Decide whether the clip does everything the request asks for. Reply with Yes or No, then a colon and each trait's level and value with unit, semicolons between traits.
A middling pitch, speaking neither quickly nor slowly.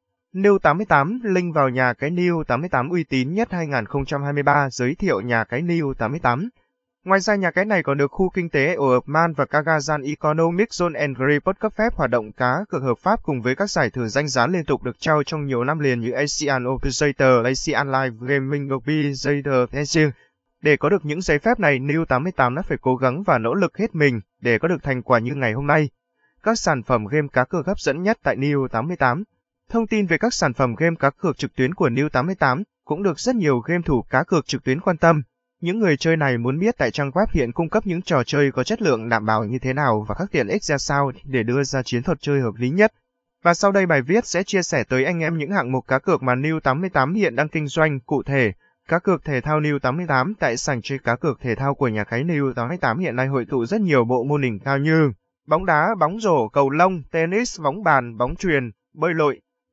Yes: medium, 145 Hz; average, 235 wpm